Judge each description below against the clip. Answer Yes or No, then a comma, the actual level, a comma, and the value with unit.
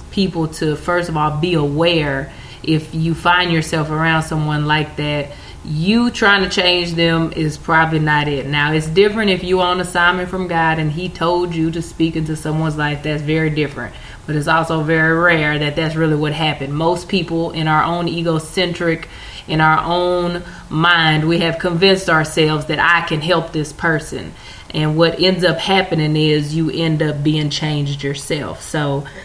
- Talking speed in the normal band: Yes, average, 180 wpm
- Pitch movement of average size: No, narrow, 2.1 semitones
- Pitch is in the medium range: Yes, medium, 160 Hz